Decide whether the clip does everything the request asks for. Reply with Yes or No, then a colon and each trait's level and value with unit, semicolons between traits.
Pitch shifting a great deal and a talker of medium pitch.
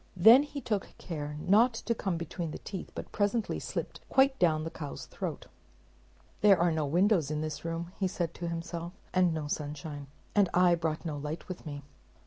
No: average, 3.8 semitones; medium, 170 Hz